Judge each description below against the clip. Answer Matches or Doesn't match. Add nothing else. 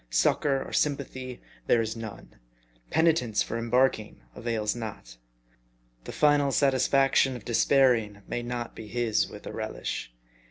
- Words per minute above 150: Doesn't match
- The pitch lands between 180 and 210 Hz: Doesn't match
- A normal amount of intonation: Matches